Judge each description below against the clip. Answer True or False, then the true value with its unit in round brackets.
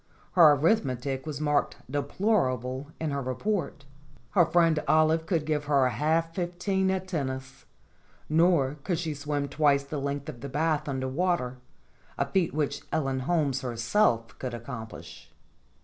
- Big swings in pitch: False (3.7 semitones)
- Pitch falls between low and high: True (145 Hz)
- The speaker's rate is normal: True (150 wpm)